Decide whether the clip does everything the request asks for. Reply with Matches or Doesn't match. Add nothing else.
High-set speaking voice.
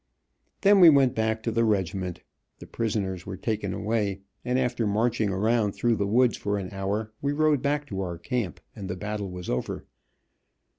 Doesn't match